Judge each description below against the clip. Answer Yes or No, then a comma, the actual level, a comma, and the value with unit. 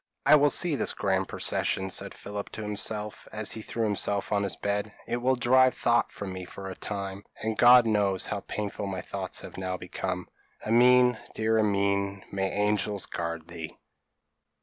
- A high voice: No, low, 105 Hz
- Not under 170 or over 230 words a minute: Yes, average, 180 wpm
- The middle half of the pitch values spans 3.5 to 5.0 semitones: No, narrow, 2.6 semitones